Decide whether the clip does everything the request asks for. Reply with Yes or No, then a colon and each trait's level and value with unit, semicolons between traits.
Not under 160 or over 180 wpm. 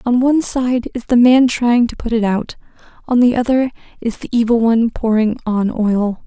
No: average, 200 wpm